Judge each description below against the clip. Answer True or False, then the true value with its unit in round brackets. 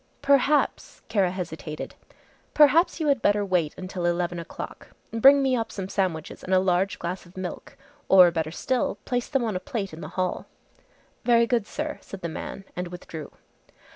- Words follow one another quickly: False (175 wpm)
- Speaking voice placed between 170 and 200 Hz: True (190 Hz)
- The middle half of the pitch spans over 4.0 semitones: True (5.5 semitones)